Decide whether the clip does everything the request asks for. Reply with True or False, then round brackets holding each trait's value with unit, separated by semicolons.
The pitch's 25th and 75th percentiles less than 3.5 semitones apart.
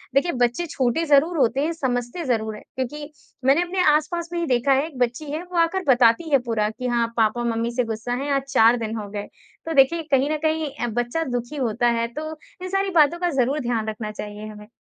False (5.1 semitones)